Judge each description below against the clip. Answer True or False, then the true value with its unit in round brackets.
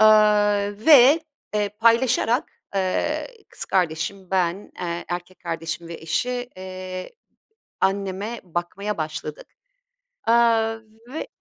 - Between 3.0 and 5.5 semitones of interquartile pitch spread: True (3.7 semitones)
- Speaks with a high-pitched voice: True (195 Hz)